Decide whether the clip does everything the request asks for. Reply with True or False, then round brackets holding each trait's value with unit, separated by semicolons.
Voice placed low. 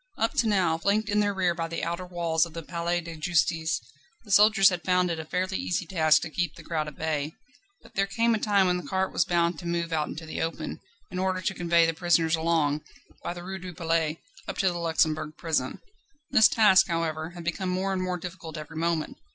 False (170 Hz)